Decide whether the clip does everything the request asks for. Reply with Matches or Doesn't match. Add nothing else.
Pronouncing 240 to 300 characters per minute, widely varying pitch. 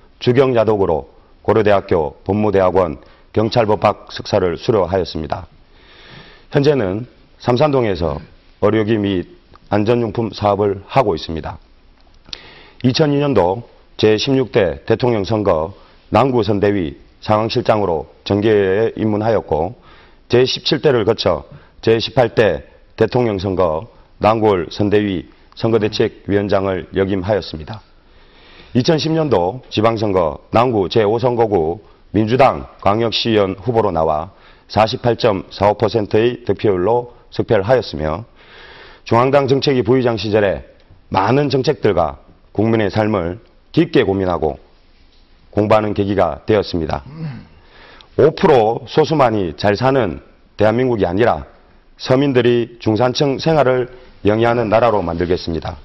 Doesn't match